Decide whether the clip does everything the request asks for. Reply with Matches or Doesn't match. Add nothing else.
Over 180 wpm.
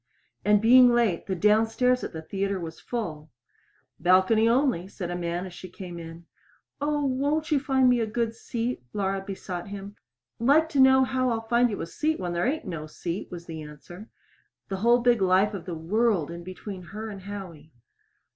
Matches